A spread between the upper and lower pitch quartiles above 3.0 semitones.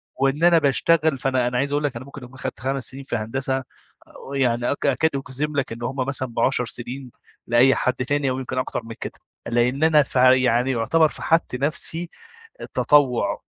No: narrow, 2.5 semitones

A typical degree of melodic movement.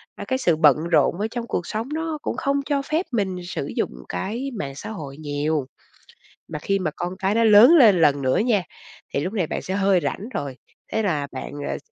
No: wide, 6.9 semitones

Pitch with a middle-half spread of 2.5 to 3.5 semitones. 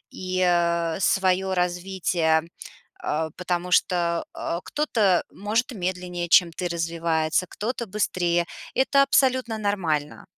Yes: average, 3.0 semitones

